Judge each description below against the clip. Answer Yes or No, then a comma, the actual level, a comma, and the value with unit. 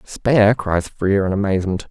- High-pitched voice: No, low, 100 Hz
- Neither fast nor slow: Yes, average, 160 wpm